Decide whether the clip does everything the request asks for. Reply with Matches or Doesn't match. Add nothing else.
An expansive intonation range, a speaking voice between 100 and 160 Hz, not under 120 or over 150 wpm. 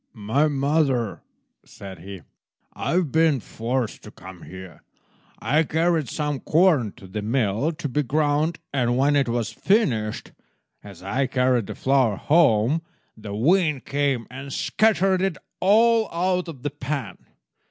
Matches